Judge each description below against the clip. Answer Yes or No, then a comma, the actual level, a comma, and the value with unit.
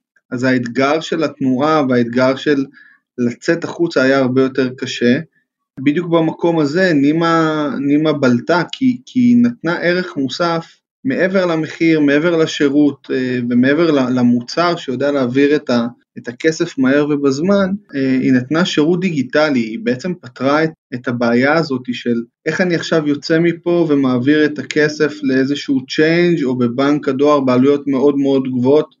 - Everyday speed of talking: Yes, average, 135 wpm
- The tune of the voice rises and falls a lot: No, average, 4.1 semitones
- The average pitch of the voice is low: No, medium, 145 Hz